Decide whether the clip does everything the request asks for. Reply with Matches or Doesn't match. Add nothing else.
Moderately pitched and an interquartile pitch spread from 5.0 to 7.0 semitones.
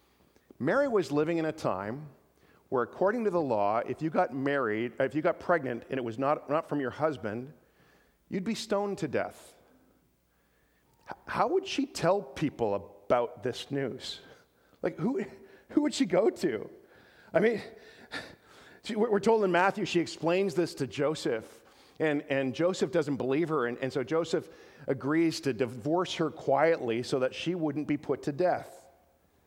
Matches